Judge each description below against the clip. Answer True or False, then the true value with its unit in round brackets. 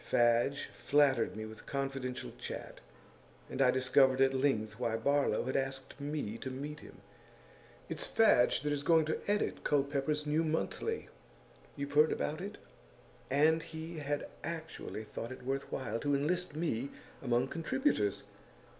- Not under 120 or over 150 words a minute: True (145 wpm)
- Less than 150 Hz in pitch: True (140 Hz)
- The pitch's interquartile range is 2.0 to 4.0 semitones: True (3.1 semitones)